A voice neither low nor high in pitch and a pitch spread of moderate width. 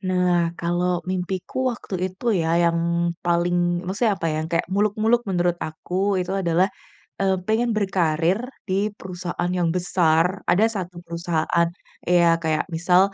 No: medium, 180 Hz; narrow, 2.1 semitones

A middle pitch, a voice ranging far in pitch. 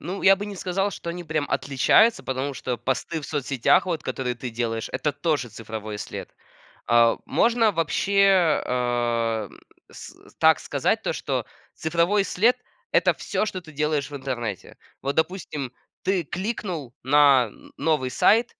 Yes: medium, 145 Hz; wide, 6.4 semitones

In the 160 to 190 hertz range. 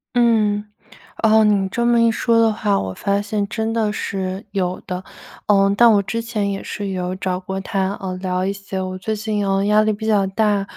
No: high, 205 Hz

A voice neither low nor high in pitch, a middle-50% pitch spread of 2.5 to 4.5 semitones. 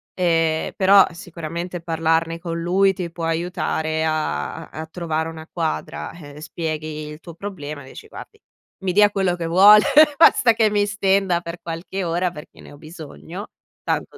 Yes: medium, 170 Hz; average, 2.8 semitones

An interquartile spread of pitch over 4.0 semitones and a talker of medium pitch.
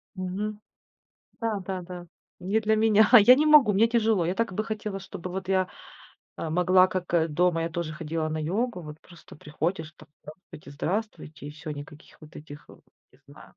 Yes: average, 4.9 semitones; medium, 180 Hz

